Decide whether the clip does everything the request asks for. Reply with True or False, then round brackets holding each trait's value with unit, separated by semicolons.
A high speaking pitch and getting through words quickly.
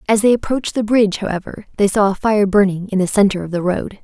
True (205 Hz; 255 wpm)